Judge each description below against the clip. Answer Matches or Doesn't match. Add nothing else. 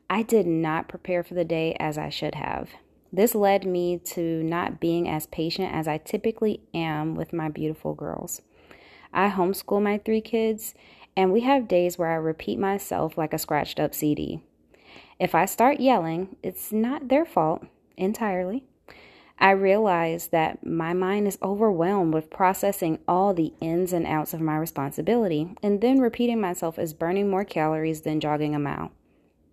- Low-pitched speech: Doesn't match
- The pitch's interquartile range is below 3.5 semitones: Doesn't match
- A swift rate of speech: Doesn't match